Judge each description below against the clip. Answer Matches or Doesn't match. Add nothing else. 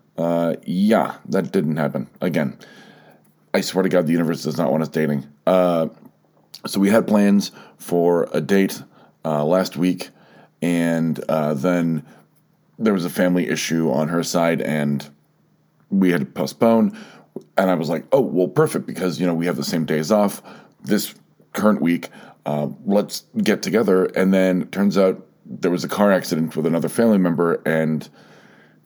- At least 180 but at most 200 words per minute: Doesn't match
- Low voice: Matches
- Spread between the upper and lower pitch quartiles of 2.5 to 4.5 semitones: Matches